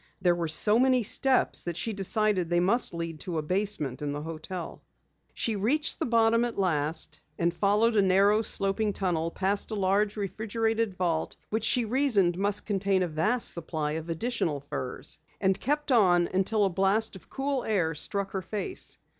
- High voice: Yes, high, 195 Hz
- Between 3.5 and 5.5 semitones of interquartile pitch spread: Yes, average, 4.3 semitones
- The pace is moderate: Yes, average, 180 wpm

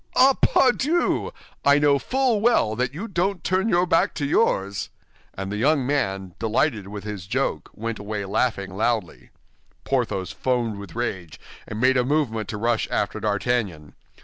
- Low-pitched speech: Yes, low, 120 Hz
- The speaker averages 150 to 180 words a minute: Yes, average, 160 wpm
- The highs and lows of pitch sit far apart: Yes, wide, 6.8 semitones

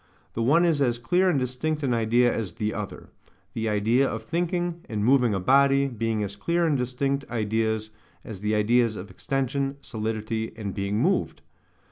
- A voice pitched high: No, low, 120 Hz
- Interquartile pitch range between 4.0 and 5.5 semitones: Yes, average, 4.3 semitones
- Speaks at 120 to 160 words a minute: No, average, 175 wpm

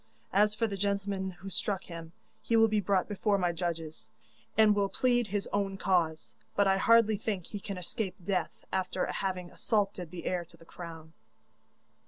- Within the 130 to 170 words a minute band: No, average, 180 wpm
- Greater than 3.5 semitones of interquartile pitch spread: No, narrow, 2.6 semitones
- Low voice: No, high, 195 Hz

